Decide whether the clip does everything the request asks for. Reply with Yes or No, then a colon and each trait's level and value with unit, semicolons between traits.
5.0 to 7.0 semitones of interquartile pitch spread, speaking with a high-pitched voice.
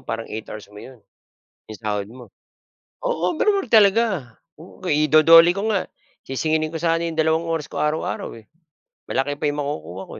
No: wide, 5.5 semitones; medium, 155 Hz